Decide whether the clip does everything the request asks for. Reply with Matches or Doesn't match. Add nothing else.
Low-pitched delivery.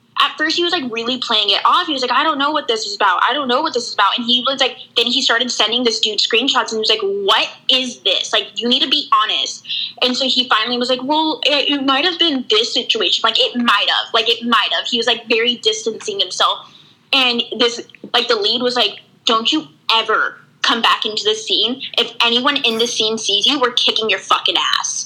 Doesn't match